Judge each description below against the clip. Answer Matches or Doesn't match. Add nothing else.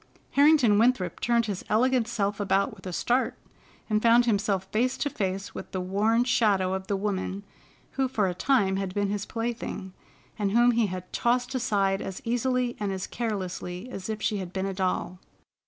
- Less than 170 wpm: Doesn't match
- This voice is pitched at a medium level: Doesn't match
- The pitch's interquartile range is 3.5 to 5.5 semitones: Matches